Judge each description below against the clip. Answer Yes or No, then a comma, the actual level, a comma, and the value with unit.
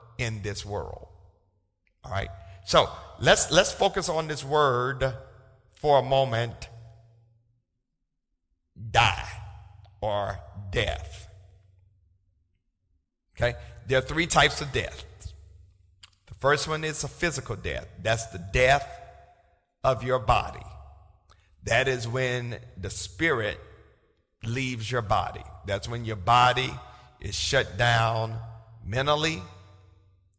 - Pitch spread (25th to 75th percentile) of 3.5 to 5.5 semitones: Yes, average, 5.0 semitones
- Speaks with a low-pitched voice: Yes, low, 110 Hz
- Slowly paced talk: Yes, slow, 105 wpm